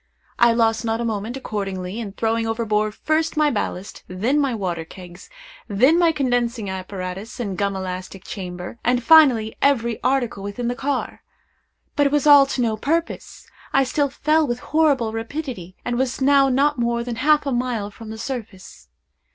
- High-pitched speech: Yes, high, 235 Hz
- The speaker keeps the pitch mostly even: No, average, 5.0 semitones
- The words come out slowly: No, average, 175 wpm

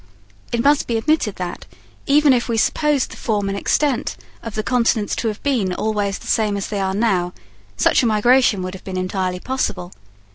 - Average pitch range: Yes, average, 4.4 semitones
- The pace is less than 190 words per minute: No, average, 195 wpm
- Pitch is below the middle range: No, high, 215 Hz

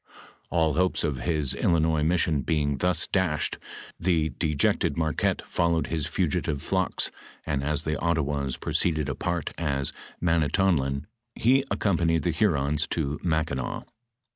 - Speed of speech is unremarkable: No, slow, 130 wpm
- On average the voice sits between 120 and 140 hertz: No, very low, 80 Hz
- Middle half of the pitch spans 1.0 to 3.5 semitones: Yes, average, 2.9 semitones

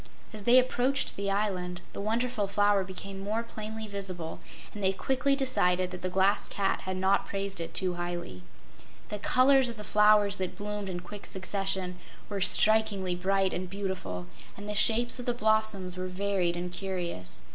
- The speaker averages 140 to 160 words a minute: No, average, 175 wpm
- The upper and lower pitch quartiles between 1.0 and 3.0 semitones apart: Yes, average, 2.7 semitones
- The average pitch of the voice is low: No, high, 195 Hz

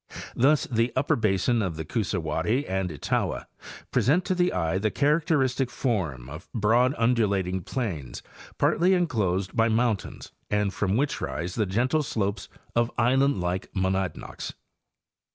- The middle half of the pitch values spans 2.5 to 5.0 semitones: No, wide, 5.6 semitones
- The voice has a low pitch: Yes, low, 110 Hz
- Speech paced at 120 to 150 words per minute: Yes, average, 140 wpm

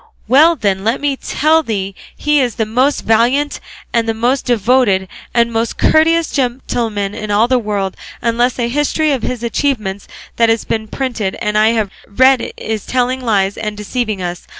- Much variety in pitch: No, average, 3.6 semitones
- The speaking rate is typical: Yes, average, 180 wpm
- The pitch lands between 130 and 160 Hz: No, high, 235 Hz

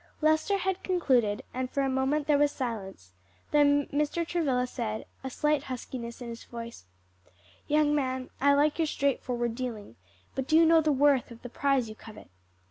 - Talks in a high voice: Yes, very high, 270 Hz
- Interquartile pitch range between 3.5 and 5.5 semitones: Yes, average, 3.8 semitones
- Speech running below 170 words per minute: No, average, 180 wpm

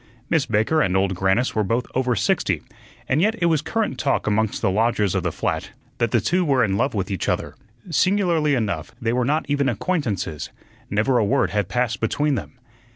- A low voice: Yes, low, 120 Hz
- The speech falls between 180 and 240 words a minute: Yes, fast, 205 wpm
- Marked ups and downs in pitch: Yes, wide, 6.0 semitones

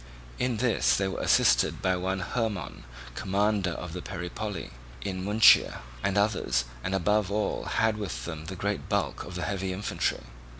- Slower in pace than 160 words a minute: No, average, 165 wpm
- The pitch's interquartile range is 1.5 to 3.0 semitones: Yes, narrow, 2.6 semitones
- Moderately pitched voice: No, very low, 95 Hz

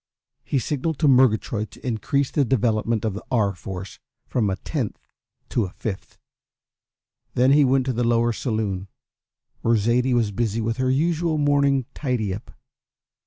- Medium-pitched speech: No, low, 120 Hz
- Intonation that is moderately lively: Yes, average, 3.8 semitones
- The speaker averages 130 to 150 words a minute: No, average, 160 wpm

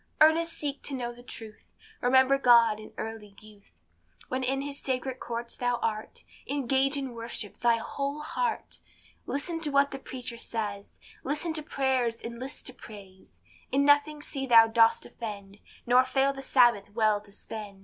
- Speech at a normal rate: Yes, average, 170 wpm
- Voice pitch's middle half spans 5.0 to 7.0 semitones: No, average, 3.6 semitones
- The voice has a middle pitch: No, very high, 250 Hz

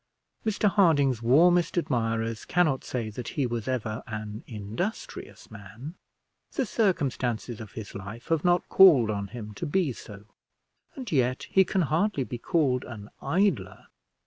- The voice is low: Yes, low, 125 Hz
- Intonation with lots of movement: Yes, wide, 7.7 semitones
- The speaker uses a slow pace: No, average, 145 wpm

